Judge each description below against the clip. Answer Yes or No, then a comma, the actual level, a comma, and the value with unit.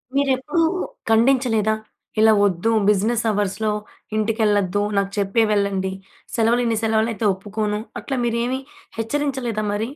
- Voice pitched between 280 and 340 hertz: No, high, 220 Hz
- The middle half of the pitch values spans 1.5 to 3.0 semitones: Yes, narrow, 2.5 semitones